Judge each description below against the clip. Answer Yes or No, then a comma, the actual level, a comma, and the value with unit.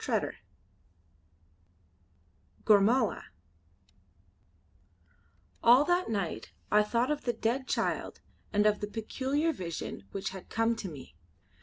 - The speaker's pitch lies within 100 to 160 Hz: No, high, 225 Hz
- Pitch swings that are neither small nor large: Yes, average, 4.3 semitones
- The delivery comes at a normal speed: No, slow, 115 wpm